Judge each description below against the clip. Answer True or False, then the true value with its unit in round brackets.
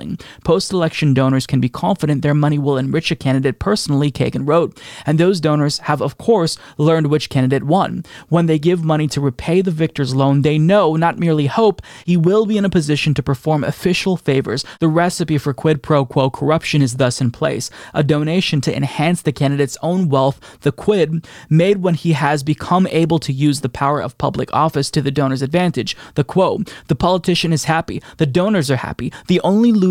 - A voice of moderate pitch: True (155 Hz)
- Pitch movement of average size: True (3.5 semitones)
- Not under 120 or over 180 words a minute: False (200 wpm)